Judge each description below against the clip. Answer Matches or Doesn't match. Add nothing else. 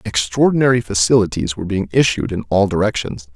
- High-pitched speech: Doesn't match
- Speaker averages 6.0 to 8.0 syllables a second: Matches